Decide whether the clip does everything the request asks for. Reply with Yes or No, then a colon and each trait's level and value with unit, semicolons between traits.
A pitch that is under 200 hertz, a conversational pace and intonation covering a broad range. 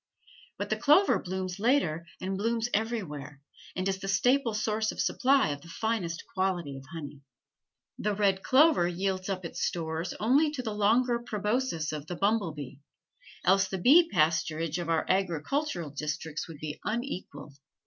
Yes: high, 190 Hz; average, 160 wpm; wide, 5.7 semitones